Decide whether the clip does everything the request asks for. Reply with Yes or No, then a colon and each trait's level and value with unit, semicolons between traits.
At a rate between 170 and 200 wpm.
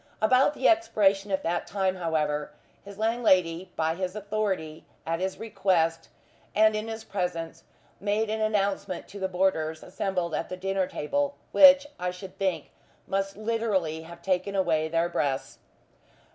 No: average, 150 wpm